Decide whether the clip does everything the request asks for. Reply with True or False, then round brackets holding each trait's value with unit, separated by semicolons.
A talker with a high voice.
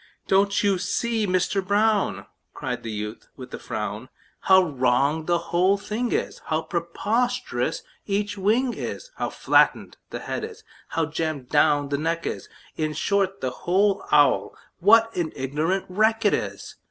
False (180 Hz)